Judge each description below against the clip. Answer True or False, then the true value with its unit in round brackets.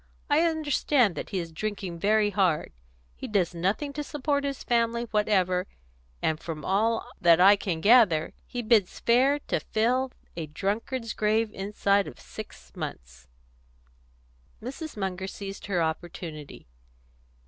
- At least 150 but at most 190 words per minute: False (135 wpm)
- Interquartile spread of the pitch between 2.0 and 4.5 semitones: False (5.1 semitones)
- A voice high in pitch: True (205 Hz)